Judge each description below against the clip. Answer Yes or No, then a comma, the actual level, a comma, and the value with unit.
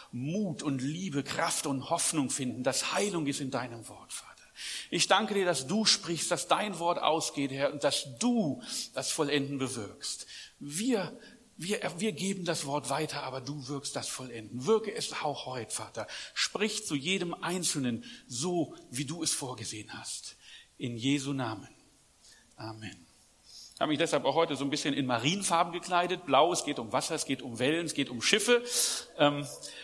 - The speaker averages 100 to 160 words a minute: No, average, 175 wpm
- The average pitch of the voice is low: No, medium, 150 Hz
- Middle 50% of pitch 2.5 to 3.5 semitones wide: No, average, 4.8 semitones